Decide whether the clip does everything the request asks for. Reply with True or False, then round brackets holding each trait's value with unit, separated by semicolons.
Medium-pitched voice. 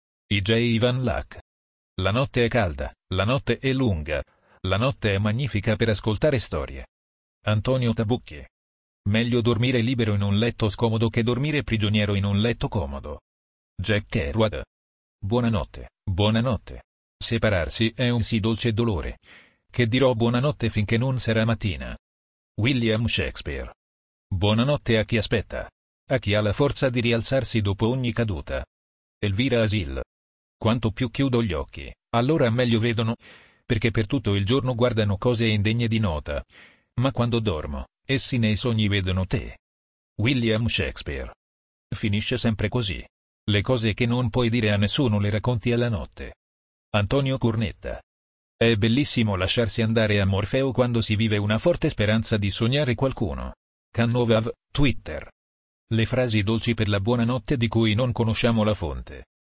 False (110 Hz)